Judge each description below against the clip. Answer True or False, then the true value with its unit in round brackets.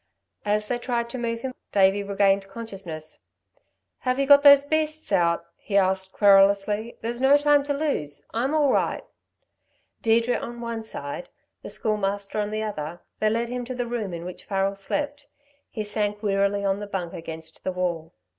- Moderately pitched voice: False (210 Hz)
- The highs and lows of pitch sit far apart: False (3.8 semitones)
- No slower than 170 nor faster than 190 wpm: True (175 wpm)